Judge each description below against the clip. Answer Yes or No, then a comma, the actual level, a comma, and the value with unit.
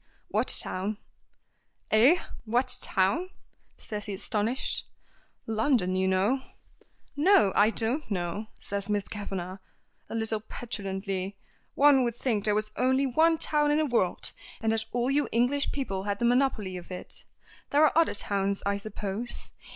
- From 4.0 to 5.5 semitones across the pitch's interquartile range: Yes, average, 4.7 semitones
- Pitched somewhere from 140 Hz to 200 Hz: No, high, 220 Hz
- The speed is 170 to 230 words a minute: No, average, 150 wpm